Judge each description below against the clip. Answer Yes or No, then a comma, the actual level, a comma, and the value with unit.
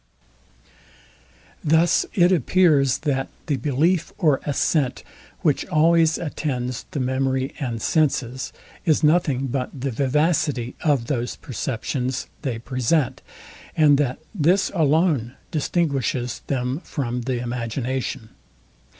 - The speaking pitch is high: No, medium, 140 Hz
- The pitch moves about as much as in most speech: Yes, average, 3.8 semitones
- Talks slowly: Yes, slow, 105 wpm